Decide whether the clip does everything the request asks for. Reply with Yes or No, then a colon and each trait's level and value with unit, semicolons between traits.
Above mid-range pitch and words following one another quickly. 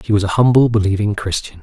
No: low, 105 Hz; fast, 220 wpm